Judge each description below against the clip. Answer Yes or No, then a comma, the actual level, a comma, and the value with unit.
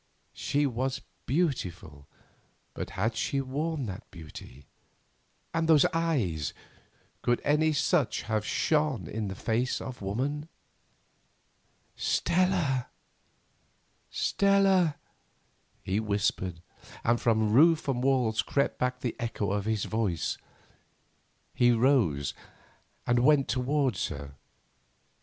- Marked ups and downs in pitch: Yes, wide, 5.8 semitones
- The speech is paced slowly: Yes, slow, 100 wpm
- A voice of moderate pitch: No, low, 120 Hz